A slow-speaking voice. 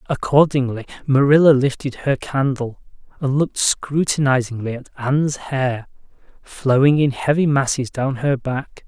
Yes: slow, 120 wpm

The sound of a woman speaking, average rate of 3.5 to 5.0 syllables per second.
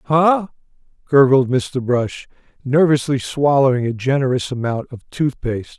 No: male; 4.6 syllables/s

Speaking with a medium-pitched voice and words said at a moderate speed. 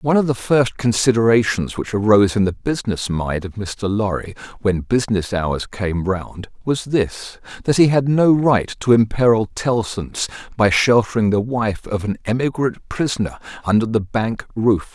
No: low, 110 Hz; average, 160 wpm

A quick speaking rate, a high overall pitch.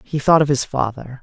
No: fast, 245 wpm; low, 135 Hz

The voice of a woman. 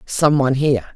Yes: female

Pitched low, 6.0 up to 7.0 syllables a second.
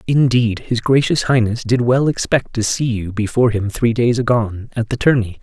No: low, 115 Hz; 5.2 syllables/s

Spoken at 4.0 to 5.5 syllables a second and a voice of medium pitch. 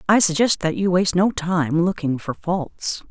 Yes: 4.5 syllables/s; medium, 175 Hz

